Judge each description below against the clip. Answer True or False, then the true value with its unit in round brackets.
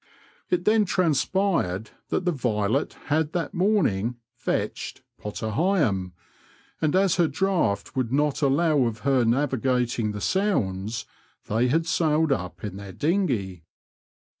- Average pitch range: False (7.6 semitones)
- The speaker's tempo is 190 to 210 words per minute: False (140 wpm)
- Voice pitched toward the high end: False (135 Hz)